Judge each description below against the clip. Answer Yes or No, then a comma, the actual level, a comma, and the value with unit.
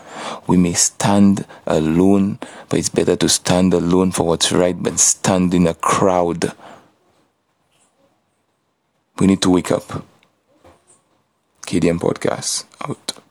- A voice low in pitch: Yes, very low, 90 Hz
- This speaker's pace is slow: Yes, slow, 115 wpm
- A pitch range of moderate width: No, narrow, 1.8 semitones